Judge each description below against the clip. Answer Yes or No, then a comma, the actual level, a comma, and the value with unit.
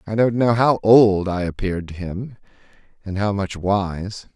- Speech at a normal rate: Yes, average, 165 wpm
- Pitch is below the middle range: Yes, low, 100 Hz